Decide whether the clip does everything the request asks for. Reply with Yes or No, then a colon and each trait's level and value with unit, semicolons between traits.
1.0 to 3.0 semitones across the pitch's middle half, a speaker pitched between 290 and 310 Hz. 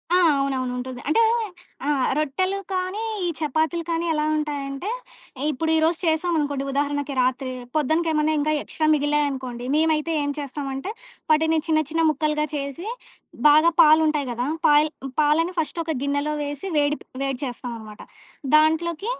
Yes: narrow, 2.4 semitones; very high, 300 Hz